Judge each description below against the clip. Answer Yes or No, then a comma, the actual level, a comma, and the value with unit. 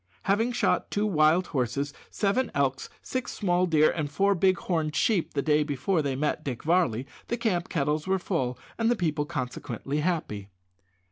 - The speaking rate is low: No, average, 175 wpm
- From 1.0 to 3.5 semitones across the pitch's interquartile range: No, average, 5.0 semitones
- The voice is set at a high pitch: No, medium, 160 Hz